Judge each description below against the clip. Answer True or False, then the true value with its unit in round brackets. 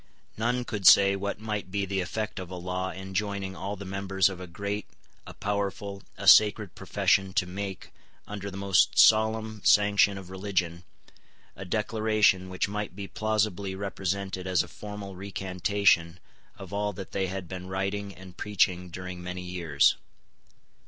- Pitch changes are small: True (1.8 semitones)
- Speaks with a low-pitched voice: True (95 Hz)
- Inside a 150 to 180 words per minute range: True (160 wpm)